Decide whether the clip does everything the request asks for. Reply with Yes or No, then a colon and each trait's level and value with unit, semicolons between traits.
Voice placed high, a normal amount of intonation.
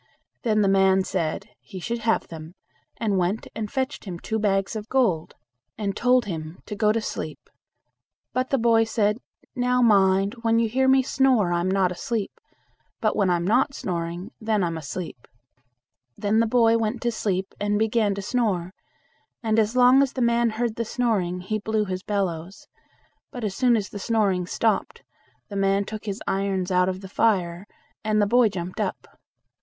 Yes: high, 210 Hz; average, 3.4 semitones